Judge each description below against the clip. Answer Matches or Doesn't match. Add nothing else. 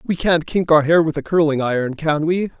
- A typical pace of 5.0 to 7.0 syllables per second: Matches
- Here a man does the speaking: Matches